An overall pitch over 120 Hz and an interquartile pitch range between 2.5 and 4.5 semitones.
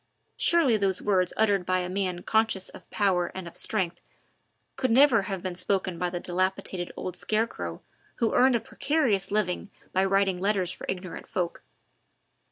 Yes: high, 190 Hz; average, 2.9 semitones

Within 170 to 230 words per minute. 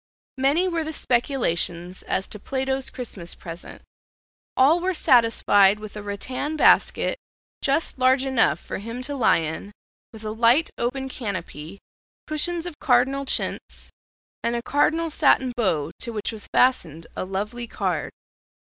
No: average, 145 wpm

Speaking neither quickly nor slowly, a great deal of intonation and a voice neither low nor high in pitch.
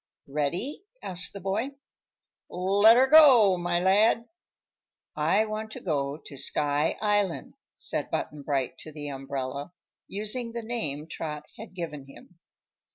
No: slow, 130 wpm; wide, 6.7 semitones; medium, 180 Hz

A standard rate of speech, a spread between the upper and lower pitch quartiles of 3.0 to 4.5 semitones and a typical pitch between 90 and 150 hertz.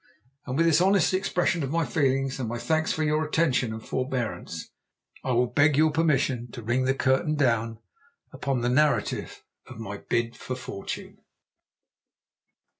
Yes: average, 160 wpm; average, 4.2 semitones; low, 135 Hz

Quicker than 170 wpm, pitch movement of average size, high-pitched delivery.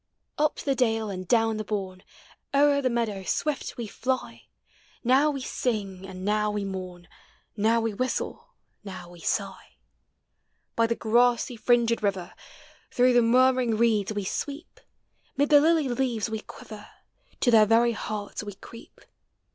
No: average, 155 wpm; average, 3.6 semitones; high, 225 Hz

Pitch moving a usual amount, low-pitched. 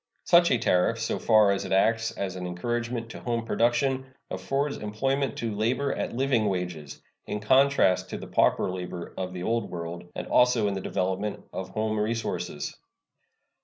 Yes: average, 4.5 semitones; low, 110 Hz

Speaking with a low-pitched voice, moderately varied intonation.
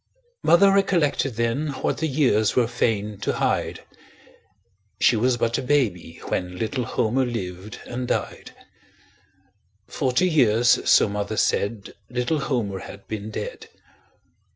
Yes: low, 120 Hz; average, 4.3 semitones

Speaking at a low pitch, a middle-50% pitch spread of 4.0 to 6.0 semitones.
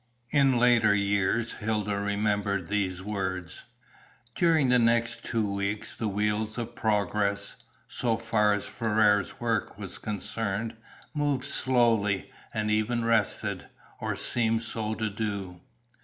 No: low, 110 Hz; narrow, 2.4 semitones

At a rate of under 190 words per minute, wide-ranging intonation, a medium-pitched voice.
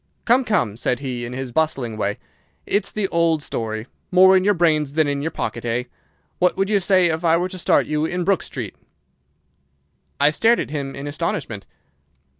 No: average, 195 wpm; wide, 5.7 semitones; medium, 155 Hz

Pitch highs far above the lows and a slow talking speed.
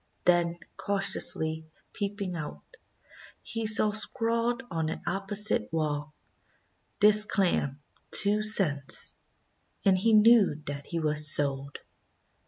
Yes: wide, 5.8 semitones; slow, 105 wpm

